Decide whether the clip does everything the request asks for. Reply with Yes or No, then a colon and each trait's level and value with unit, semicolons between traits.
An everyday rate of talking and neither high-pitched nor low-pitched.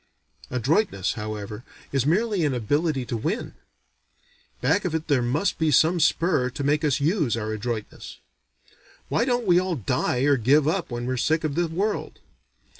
Yes: average, 170 wpm; medium, 145 Hz